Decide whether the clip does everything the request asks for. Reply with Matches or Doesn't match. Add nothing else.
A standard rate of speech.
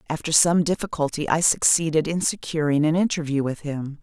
Matches